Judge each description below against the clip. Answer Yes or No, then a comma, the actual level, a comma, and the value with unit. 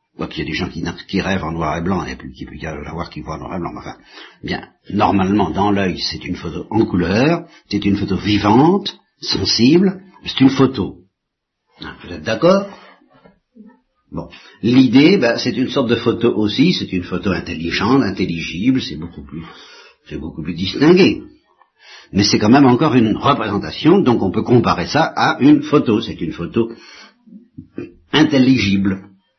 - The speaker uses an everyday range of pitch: No, wide, 7.3 semitones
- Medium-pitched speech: No, low, 100 Hz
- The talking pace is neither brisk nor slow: Yes, average, 180 wpm